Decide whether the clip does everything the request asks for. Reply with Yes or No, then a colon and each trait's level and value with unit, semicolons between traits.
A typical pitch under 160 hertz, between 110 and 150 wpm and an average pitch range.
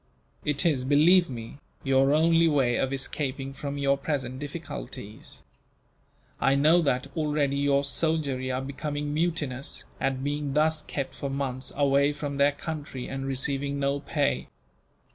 No: medium, 140 Hz; average, 145 wpm; narrow, 1.7 semitones